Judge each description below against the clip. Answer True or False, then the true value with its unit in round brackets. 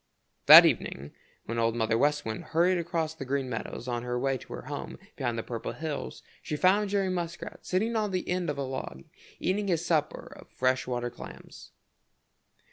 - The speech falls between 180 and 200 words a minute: True (190 wpm)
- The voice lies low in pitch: False (145 Hz)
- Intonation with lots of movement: True (6.7 semitones)